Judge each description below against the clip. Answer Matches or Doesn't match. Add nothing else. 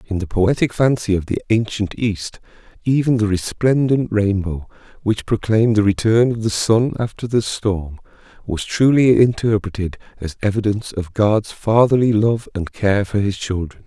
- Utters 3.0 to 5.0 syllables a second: Matches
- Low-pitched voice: Matches